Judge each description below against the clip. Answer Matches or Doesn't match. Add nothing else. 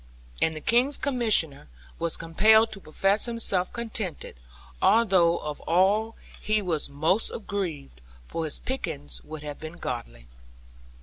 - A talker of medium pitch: Matches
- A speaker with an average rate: Doesn't match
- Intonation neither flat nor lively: Doesn't match